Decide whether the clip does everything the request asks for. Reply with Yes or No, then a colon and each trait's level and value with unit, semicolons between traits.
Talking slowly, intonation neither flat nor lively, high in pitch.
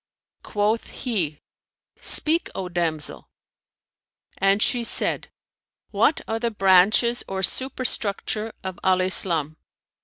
Yes: slow, 100 wpm; average, 3.9 semitones; high, 195 Hz